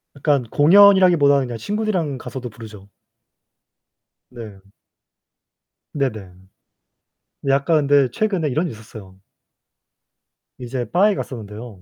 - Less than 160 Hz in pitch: Yes, low, 135 Hz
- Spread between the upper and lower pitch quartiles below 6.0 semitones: No, wide, 6.3 semitones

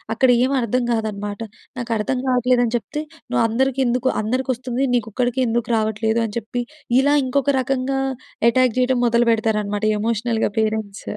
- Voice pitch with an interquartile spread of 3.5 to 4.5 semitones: No, narrow, 2.6 semitones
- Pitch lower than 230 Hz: No, high, 235 Hz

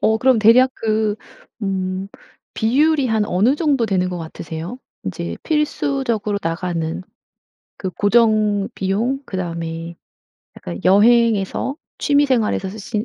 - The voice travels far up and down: No, average, 4.6 semitones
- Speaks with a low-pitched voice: No, high, 210 Hz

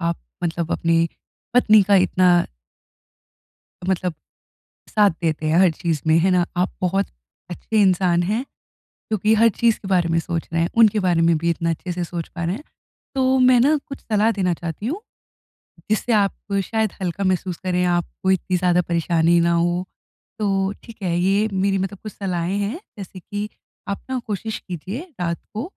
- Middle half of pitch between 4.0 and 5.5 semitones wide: No, average, 3.5 semitones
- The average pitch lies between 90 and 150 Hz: No, medium, 185 Hz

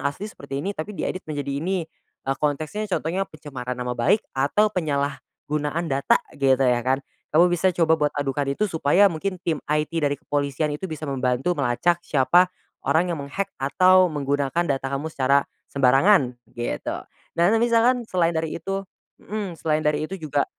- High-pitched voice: No, medium, 155 Hz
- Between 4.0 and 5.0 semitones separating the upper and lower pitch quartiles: Yes, average, 4.3 semitones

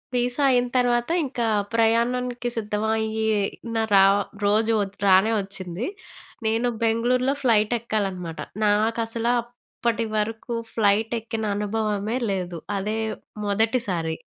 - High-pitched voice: Yes, high, 225 Hz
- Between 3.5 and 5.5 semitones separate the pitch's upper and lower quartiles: No, narrow, 2.4 semitones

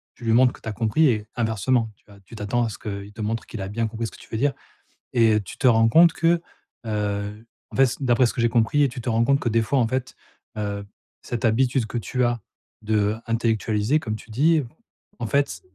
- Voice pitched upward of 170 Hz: No, low, 115 Hz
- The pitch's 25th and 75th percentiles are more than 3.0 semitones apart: No, average, 2.7 semitones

